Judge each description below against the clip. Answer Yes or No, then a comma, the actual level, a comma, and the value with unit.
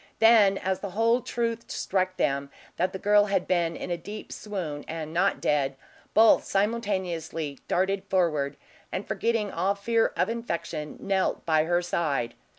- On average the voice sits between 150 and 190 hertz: Yes, medium, 185 Hz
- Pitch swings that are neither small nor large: Yes, average, 4.1 semitones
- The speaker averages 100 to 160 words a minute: Yes, average, 155 wpm